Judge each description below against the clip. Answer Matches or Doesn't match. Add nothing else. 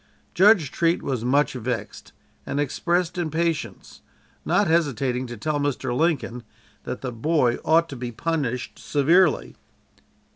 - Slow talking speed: Matches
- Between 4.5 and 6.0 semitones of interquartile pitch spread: Matches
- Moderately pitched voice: Matches